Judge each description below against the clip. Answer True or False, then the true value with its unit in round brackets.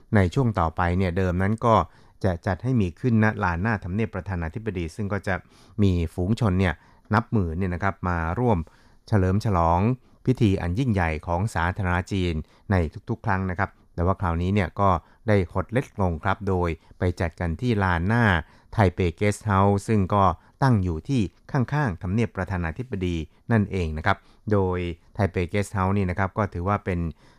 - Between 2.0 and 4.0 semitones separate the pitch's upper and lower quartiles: True (3.4 semitones)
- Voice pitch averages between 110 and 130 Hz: False (95 Hz)